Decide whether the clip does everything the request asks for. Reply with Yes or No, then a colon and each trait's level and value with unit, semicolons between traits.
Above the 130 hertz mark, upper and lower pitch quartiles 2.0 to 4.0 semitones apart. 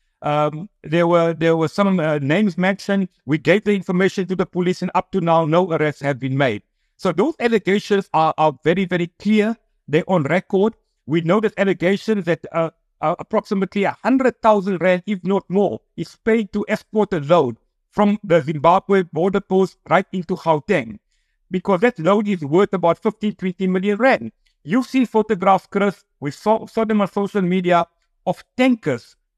Yes: high, 190 Hz; average, 3.5 semitones